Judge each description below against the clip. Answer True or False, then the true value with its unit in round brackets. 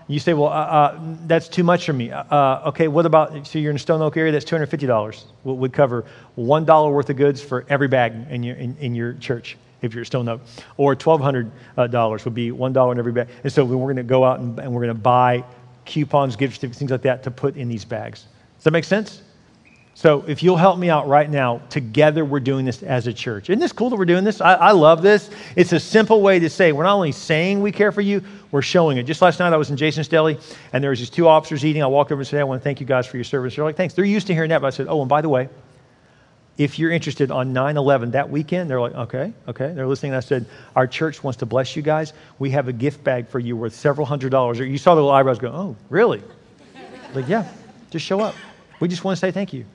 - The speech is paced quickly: True (270 wpm)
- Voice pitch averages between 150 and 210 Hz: False (140 Hz)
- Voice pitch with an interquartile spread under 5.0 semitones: True (4.0 semitones)